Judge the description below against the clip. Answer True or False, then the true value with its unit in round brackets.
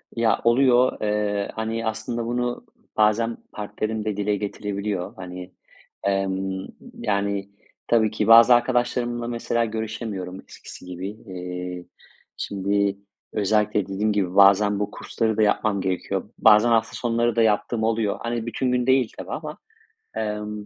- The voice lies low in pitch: True (105 Hz)